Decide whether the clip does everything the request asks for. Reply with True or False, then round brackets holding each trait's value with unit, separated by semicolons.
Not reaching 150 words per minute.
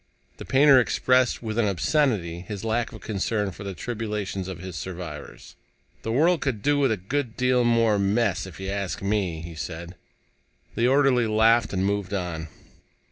False (175 wpm)